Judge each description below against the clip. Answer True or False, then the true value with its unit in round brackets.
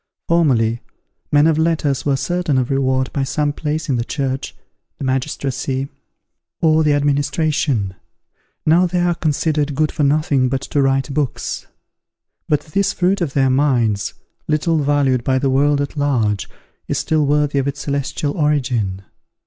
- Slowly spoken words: False (155 wpm)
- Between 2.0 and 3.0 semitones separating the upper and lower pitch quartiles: True (2.5 semitones)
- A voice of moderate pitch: True (145 Hz)